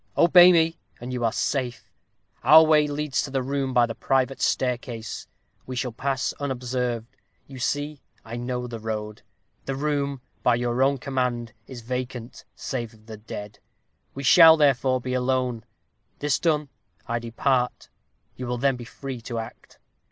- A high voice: No, low, 130 Hz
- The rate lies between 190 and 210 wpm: No, average, 160 wpm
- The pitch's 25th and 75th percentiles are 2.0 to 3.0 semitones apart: Yes, narrow, 2.6 semitones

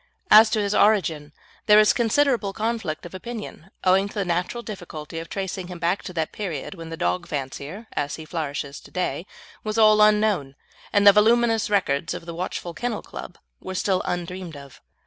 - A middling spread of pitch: Yes, average, 4.4 semitones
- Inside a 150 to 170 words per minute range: No, average, 185 wpm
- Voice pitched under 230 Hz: Yes, medium, 185 Hz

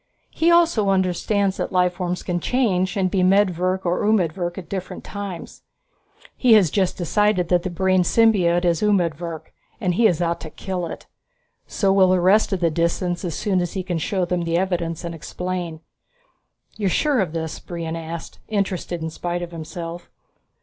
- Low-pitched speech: No, medium, 180 Hz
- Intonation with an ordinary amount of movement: No, narrow, 2.3 semitones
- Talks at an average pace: Yes, average, 180 wpm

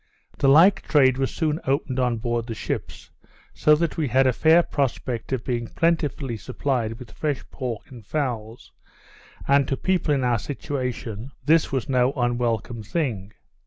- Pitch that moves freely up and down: No, average, 3.7 semitones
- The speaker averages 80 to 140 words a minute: No, average, 165 wpm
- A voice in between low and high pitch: No, low, 130 Hz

